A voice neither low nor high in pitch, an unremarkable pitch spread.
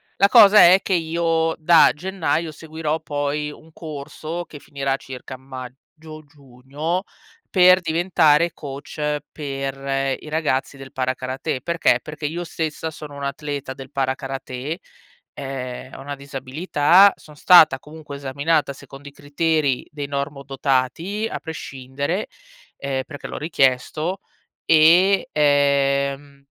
Yes: medium, 145 Hz; average, 3.0 semitones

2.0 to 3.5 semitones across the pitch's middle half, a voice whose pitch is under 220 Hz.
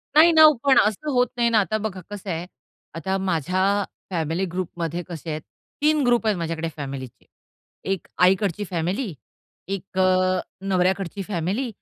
No: average, 4.1 semitones; medium, 185 Hz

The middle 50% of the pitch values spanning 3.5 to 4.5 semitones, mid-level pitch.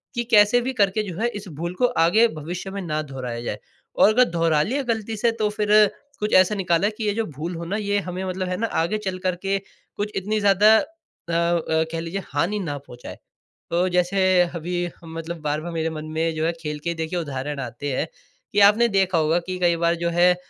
Yes: average, 4.2 semitones; medium, 180 Hz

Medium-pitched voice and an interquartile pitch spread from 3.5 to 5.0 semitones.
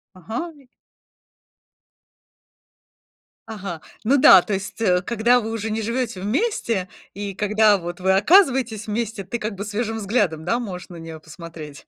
No: high, 210 Hz; average, 3.9 semitones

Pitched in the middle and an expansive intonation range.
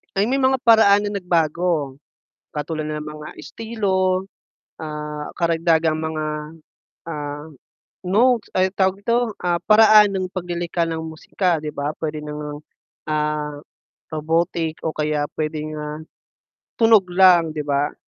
No: medium, 165 Hz; average, 3.7 semitones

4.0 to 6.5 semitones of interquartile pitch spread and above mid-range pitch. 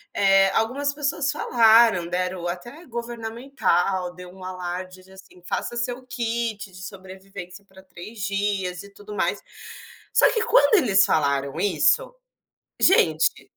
Yes: average, 4.4 semitones; high, 195 Hz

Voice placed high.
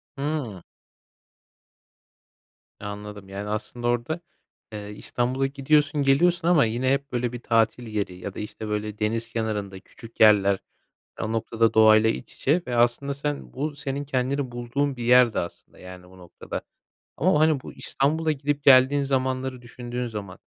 No: low, 120 Hz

